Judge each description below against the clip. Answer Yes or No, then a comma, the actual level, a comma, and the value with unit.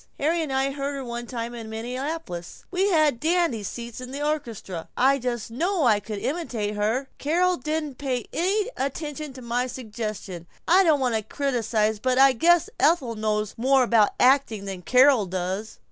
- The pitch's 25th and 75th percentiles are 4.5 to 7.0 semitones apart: Yes, average, 5.1 semitones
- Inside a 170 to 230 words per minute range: Yes, average, 175 wpm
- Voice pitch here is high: Yes, very high, 255 Hz